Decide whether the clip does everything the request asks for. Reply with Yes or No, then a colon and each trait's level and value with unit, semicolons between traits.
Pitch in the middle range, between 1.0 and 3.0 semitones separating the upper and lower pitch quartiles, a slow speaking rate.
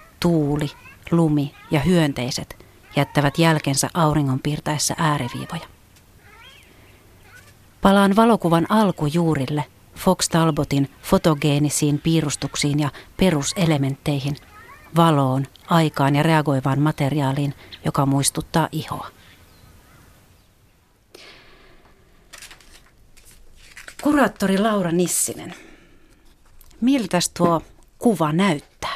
No: medium, 150 Hz; average, 3.8 semitones; slow, 65 wpm